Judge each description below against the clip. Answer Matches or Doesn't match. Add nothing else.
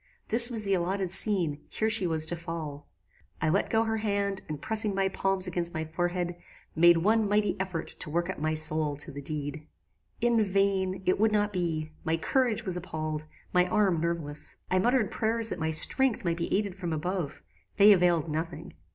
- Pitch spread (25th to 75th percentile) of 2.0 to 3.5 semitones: Doesn't match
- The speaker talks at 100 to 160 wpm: Doesn't match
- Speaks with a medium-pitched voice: Matches